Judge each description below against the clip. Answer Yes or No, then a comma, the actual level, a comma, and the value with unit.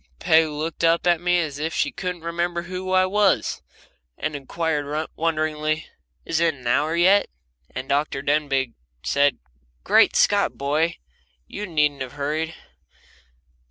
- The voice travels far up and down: No, average, 2.9 semitones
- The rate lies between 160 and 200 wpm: No, average, 140 wpm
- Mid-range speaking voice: Yes, medium, 155 Hz